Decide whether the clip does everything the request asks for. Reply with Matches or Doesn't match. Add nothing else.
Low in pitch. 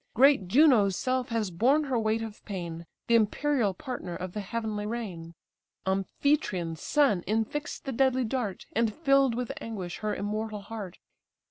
Doesn't match